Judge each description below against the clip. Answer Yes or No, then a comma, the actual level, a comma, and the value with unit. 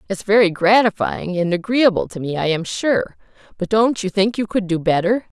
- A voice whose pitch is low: No, high, 200 Hz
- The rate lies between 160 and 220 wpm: Yes, average, 200 wpm